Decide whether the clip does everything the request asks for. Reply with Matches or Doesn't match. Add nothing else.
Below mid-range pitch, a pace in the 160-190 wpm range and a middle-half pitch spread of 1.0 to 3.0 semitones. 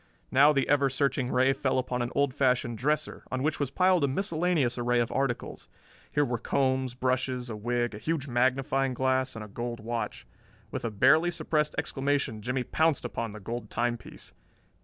Matches